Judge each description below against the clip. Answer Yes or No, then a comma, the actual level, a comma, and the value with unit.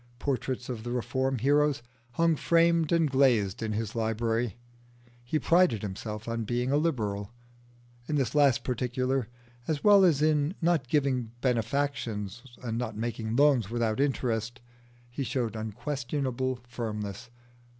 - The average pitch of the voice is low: Yes, low, 125 Hz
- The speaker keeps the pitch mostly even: No, average, 4.2 semitones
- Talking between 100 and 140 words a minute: Yes, slow, 135 wpm